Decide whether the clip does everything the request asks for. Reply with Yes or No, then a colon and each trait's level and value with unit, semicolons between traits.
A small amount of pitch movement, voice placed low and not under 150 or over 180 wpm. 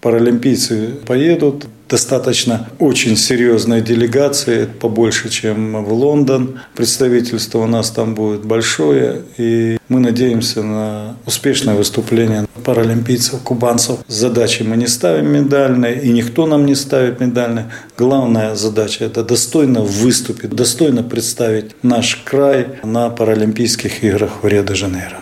No: narrow, 2.0 semitones; low, 115 Hz; average, 115 wpm